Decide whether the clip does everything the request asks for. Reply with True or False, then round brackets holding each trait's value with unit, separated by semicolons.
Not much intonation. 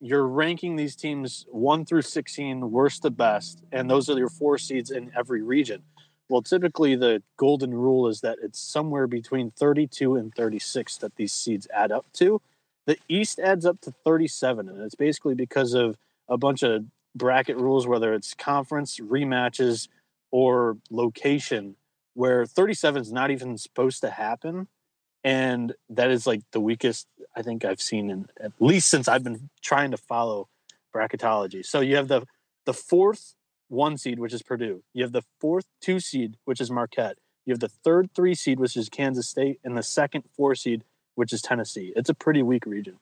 False (3.7 semitones)